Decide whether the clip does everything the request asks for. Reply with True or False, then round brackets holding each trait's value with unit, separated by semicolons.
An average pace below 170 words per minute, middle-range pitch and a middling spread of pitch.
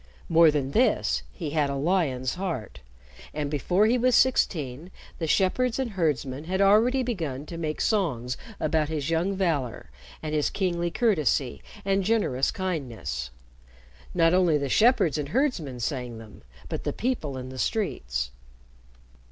False (150 wpm; 160 Hz; 6.5 semitones)